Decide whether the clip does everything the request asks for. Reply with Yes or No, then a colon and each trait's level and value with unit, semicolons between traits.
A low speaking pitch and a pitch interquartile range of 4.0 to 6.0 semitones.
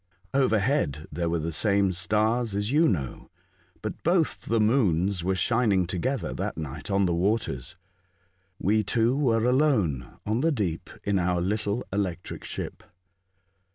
Yes: low, 100 Hz; average, 5.0 semitones